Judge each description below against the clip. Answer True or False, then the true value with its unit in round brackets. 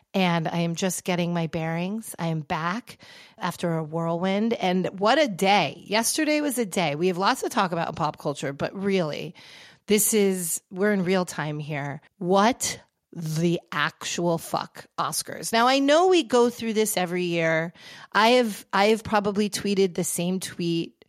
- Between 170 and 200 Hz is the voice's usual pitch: True (185 Hz)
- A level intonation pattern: False (4.0 semitones)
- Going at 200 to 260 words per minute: False (175 wpm)